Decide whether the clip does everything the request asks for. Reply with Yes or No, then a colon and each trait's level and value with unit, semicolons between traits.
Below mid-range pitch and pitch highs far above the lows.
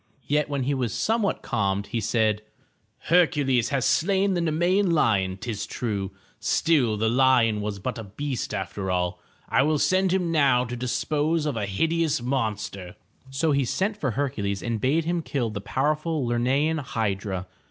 Yes: low, 130 Hz; wide, 6.3 semitones